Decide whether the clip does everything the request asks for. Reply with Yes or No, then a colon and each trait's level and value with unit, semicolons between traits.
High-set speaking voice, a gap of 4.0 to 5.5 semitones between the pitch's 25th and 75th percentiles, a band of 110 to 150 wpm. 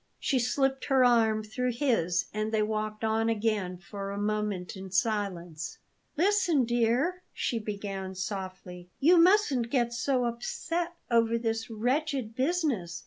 Yes: high, 225 Hz; average, 4.4 semitones; average, 140 wpm